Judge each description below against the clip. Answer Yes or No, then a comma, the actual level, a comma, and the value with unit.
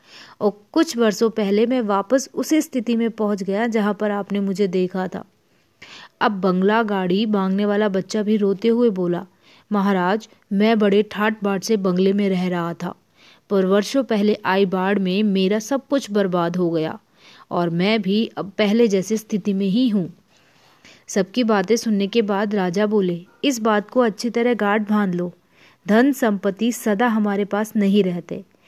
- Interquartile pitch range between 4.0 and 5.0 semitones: No, narrow, 2.5 semitones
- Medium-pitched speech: No, high, 205 Hz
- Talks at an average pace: Yes, average, 170 wpm